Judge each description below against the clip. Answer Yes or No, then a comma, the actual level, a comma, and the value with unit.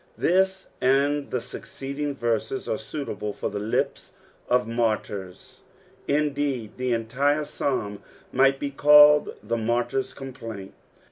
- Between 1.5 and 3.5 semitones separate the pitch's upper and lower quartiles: No, average, 4.1 semitones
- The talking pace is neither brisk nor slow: No, slow, 120 wpm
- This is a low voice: Yes, low, 130 Hz